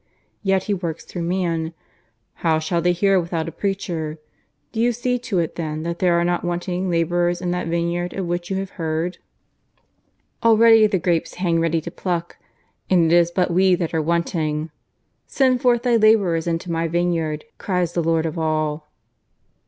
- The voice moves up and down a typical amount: No, narrow, 2.3 semitones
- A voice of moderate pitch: Yes, medium, 175 Hz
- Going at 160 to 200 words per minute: Yes, average, 180 wpm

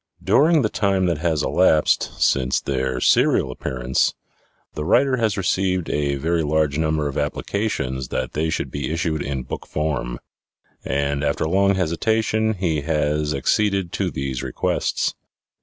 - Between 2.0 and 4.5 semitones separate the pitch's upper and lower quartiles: No, average, 5.2 semitones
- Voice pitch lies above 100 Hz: No, very low, 80 Hz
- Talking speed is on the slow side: No, average, 145 wpm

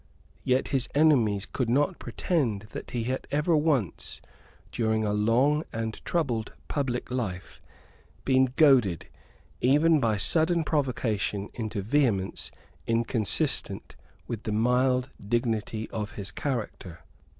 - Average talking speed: No, slow, 115 wpm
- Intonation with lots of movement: No, average, 4.6 semitones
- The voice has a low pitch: Yes, low, 120 Hz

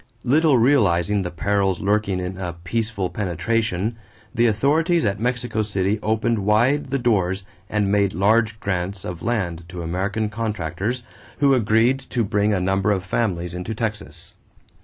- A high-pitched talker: No, low, 105 Hz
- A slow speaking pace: No, average, 150 wpm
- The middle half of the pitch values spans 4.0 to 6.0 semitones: No, average, 3.5 semitones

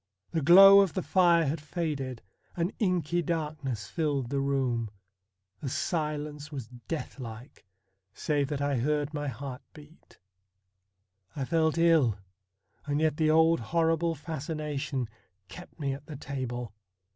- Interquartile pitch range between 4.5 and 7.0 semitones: No, average, 3.2 semitones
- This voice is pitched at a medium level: Yes, medium, 150 Hz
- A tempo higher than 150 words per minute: No, slow, 135 wpm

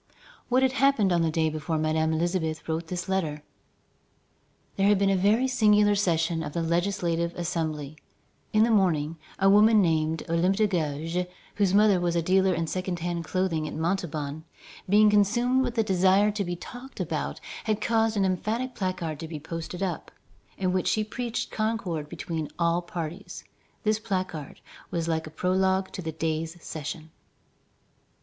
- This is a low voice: No, medium, 180 Hz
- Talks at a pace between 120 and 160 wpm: No, average, 170 wpm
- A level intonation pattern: No, average, 4.1 semitones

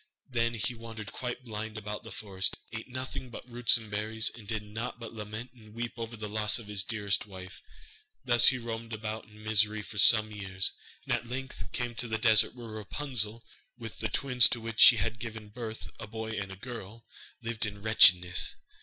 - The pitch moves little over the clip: Yes, narrow, 1.8 semitones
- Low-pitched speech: Yes, low, 110 Hz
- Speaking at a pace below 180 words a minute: No, average, 200 wpm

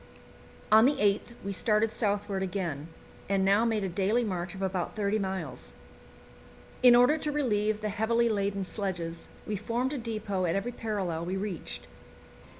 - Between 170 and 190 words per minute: No, average, 160 wpm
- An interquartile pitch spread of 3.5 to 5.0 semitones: No, average, 2.9 semitones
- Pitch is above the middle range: Yes, high, 205 Hz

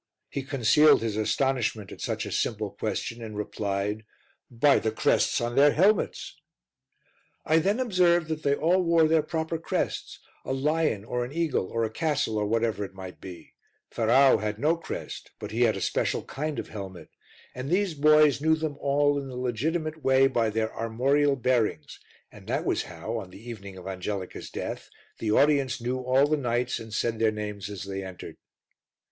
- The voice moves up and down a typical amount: No, wide, 5.8 semitones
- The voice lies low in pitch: Yes, low, 125 Hz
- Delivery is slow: No, average, 185 wpm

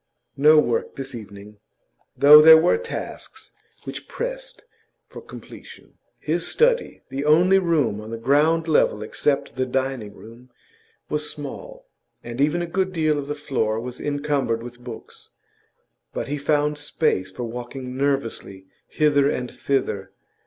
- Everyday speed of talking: Yes, average, 145 wpm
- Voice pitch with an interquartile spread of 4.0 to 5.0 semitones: Yes, average, 4.4 semitones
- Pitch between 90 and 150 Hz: Yes, medium, 140 Hz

